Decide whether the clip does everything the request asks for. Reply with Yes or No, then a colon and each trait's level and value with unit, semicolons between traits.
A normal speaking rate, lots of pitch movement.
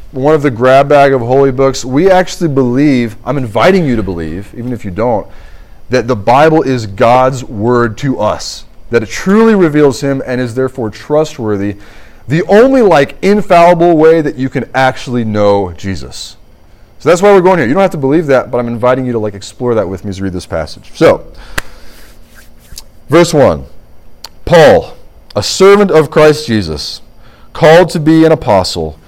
Yes: average, 185 wpm; wide, 6.3 semitones